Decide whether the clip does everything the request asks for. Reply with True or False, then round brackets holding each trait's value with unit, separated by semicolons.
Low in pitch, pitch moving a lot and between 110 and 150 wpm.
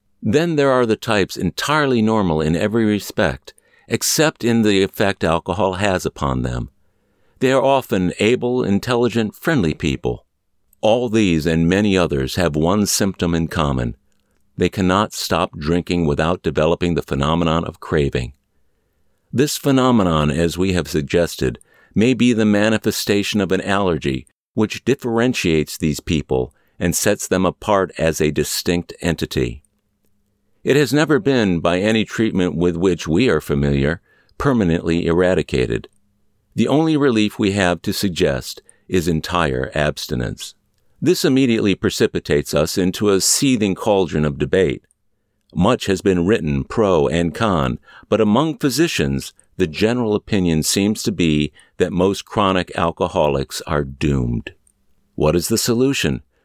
True (95 Hz; 5.7 semitones; 140 wpm)